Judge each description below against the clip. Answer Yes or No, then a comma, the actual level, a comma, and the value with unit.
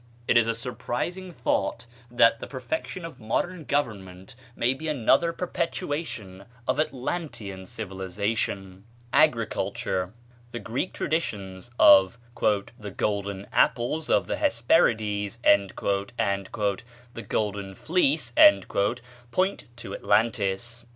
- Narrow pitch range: No, wide, 5.5 semitones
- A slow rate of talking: Yes, slow, 105 wpm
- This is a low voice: Yes, low, 115 Hz